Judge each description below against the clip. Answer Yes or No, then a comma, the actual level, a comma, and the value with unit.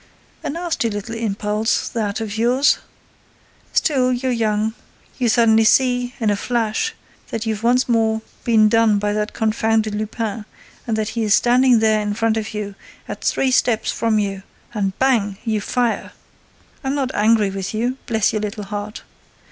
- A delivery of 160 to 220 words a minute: No, average, 150 wpm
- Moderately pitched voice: No, high, 220 Hz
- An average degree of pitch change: No, narrow, 2.3 semitones